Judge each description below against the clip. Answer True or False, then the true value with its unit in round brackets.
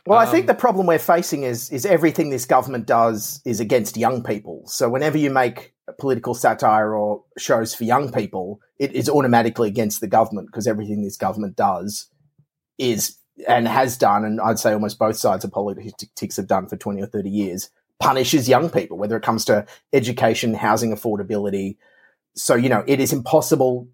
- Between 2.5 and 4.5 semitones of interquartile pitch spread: False (5.4 semitones)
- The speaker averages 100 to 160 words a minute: False (190 wpm)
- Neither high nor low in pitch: False (120 Hz)